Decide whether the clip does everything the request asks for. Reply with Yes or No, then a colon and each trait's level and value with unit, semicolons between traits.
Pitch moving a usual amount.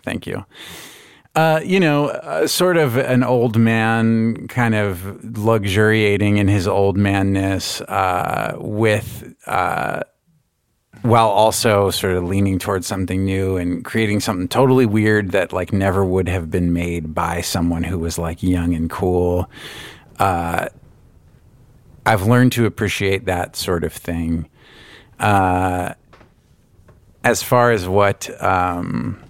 Yes: average, 3.8 semitones